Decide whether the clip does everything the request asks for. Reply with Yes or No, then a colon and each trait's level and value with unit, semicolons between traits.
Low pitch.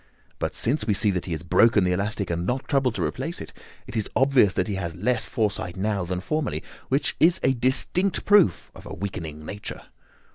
Yes: low, 105 Hz